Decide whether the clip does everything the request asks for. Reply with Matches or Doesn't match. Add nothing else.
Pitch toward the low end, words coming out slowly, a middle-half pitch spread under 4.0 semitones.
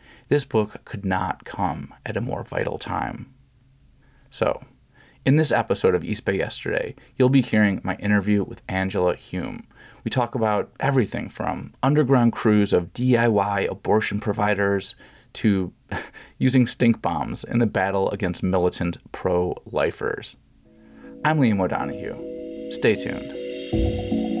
Doesn't match